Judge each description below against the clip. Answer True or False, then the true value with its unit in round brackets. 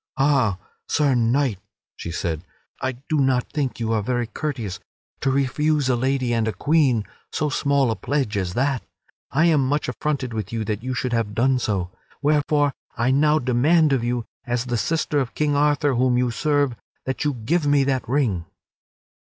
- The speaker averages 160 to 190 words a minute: True (185 wpm)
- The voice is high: False (130 Hz)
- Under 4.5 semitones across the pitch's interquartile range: True (3.7 semitones)